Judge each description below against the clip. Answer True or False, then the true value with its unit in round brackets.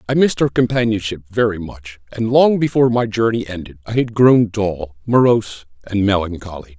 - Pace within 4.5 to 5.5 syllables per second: True (5.4 syllables/s)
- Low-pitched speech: True (105 Hz)